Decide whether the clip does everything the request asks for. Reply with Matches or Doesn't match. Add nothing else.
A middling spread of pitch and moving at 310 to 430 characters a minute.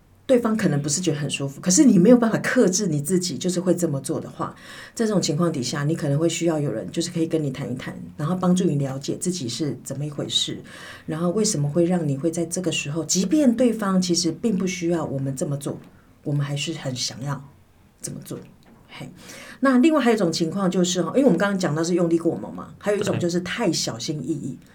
Matches